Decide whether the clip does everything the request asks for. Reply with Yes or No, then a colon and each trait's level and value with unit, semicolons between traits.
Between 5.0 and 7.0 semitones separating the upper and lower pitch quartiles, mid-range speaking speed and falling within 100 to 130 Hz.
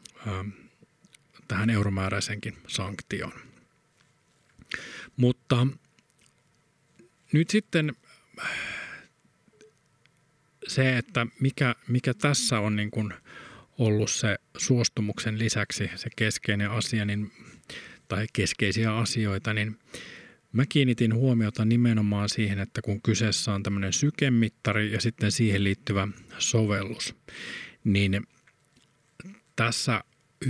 No: average, 5.3 semitones; slow, 85 wpm; low, 115 Hz